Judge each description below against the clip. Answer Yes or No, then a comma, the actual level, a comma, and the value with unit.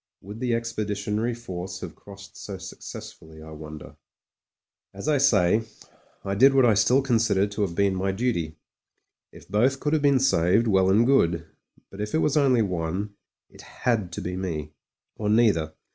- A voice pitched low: Yes, low, 105 Hz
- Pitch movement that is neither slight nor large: Yes, average, 4.6 semitones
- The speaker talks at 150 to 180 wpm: Yes, average, 175 wpm